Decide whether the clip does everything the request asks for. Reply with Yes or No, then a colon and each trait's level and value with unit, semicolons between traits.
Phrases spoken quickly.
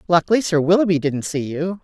No: average, 195 wpm